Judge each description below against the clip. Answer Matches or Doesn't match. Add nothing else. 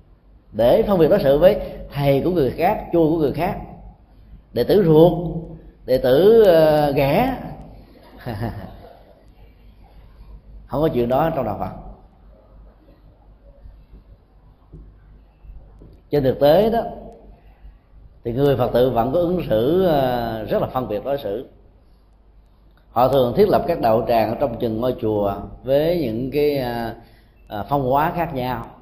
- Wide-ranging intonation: Matches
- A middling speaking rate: Doesn't match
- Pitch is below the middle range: Matches